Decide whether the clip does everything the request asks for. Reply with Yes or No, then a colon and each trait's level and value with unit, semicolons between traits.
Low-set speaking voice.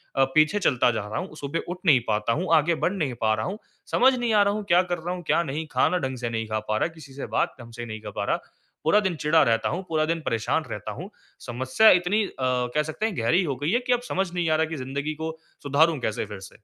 No: medium, 155 Hz